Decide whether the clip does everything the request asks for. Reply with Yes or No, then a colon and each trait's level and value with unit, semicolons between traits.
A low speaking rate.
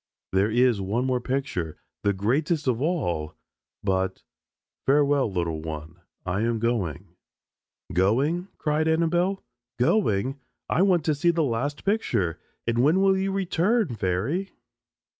Yes: slow, 130 wpm